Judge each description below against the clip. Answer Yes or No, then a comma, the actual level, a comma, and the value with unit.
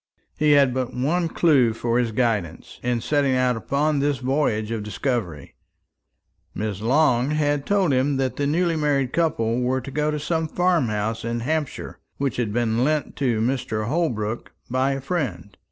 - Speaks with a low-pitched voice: Yes, low, 130 Hz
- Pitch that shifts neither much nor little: Yes, average, 4.4 semitones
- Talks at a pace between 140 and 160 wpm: No, average, 170 wpm